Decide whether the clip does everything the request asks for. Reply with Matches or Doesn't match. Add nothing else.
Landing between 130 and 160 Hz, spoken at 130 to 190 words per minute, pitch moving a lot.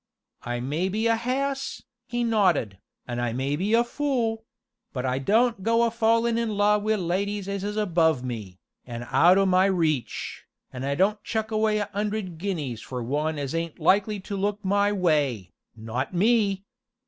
Doesn't match